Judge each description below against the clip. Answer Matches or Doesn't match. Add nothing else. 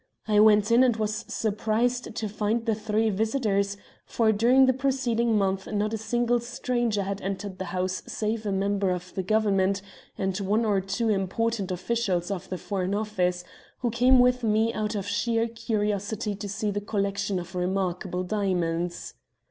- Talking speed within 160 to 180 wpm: Matches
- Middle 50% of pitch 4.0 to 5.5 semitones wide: Doesn't match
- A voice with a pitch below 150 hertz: Doesn't match